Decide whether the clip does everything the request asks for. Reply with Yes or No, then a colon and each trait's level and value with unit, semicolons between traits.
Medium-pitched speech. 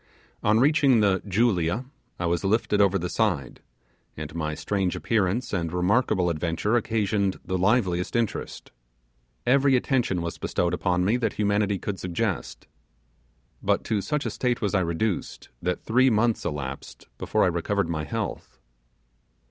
No: low, 100 Hz